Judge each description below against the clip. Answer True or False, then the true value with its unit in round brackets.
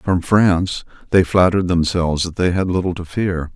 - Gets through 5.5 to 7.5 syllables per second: False (5.3 syllables/s)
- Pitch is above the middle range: False (90 Hz)